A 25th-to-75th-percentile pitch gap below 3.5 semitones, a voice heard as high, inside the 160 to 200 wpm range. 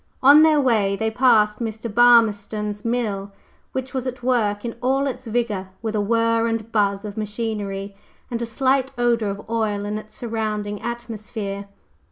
Yes: average, 2.7 semitones; high, 225 Hz; average, 165 wpm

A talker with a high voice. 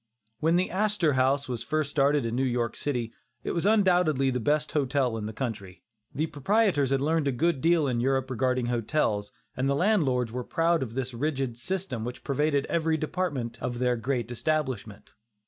No: low, 135 Hz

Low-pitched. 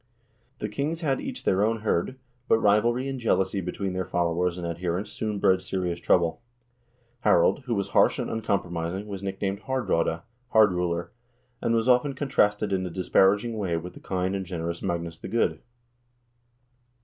Yes: very low, 95 Hz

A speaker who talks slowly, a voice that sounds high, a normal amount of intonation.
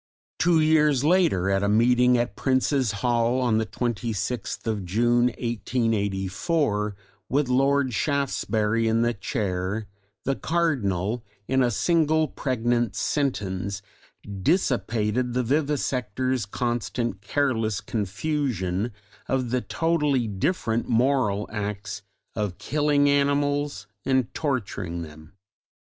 No: slow, 105 wpm; low, 120 Hz; average, 4.9 semitones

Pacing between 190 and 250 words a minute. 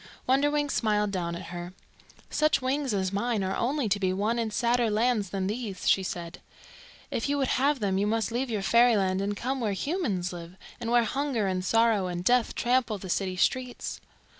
Yes: average, 195 wpm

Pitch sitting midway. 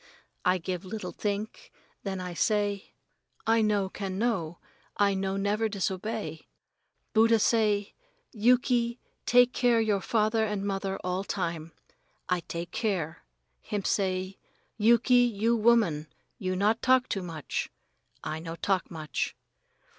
No: high, 200 Hz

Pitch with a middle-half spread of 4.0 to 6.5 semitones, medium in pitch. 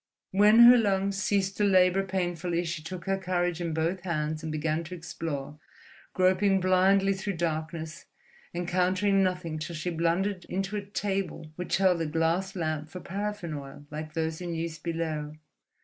No: average, 3.1 semitones; medium, 175 Hz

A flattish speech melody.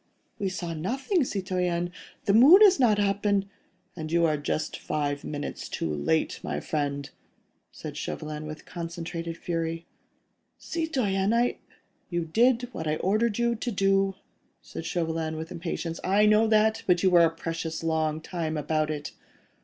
No: average, 4.7 semitones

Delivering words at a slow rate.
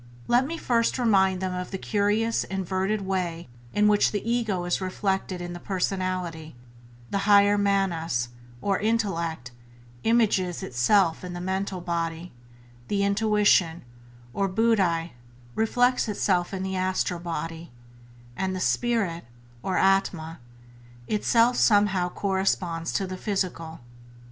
Yes: slow, 125 wpm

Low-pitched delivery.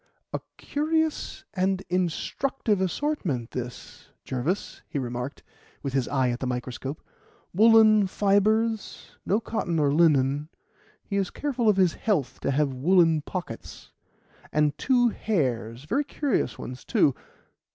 No: medium, 175 Hz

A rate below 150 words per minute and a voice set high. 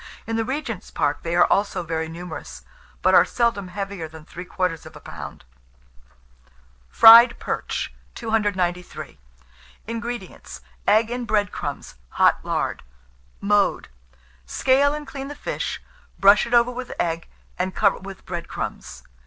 Yes: average, 140 wpm; high, 200 Hz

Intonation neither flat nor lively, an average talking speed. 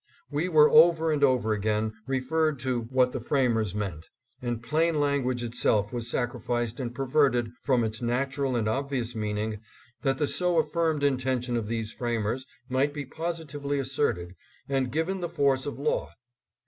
Yes: average, 3.6 semitones; average, 175 wpm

